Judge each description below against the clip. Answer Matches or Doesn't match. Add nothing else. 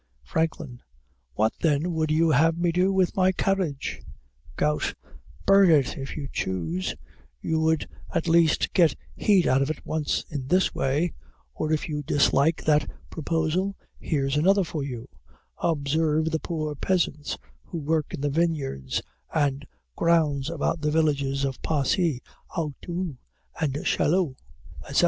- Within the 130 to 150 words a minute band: Matches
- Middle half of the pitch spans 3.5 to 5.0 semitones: Doesn't match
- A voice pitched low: Doesn't match